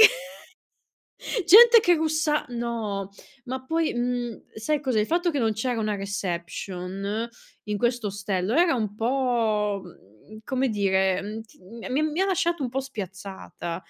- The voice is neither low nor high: No, high, 225 Hz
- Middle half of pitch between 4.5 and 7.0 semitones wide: Yes, average, 5.2 semitones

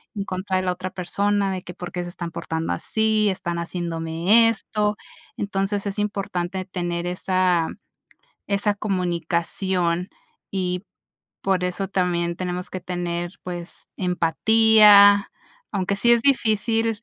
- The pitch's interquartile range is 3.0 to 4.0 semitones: No, narrow, 2.5 semitones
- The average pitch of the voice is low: No, medium, 185 Hz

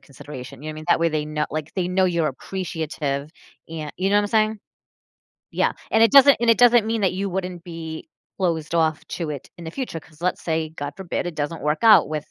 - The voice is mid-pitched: Yes, medium, 165 Hz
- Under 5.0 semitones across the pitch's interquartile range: Yes, average, 3.9 semitones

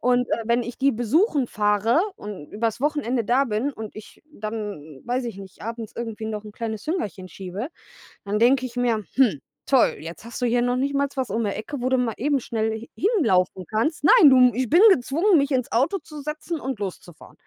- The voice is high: Yes, high, 240 Hz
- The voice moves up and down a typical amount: Yes, average, 4.2 semitones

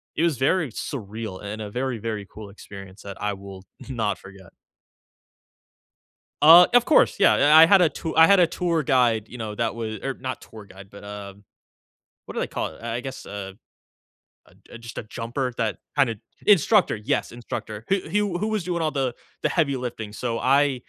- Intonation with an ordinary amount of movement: No, wide, 6.6 semitones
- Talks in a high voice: No, low, 120 Hz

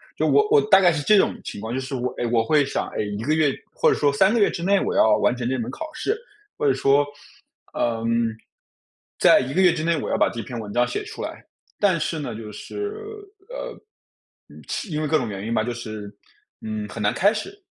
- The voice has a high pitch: No, medium, 140 Hz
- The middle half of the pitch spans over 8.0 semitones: Yes, wide, 8.8 semitones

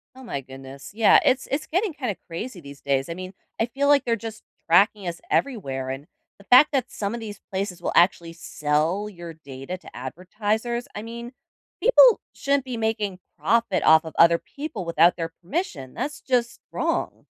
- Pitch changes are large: Yes, wide, 6.4 semitones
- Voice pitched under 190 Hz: No, high, 200 Hz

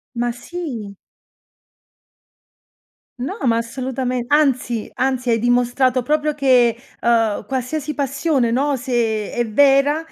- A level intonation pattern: No, average, 3.0 semitones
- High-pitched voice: Yes, very high, 255 Hz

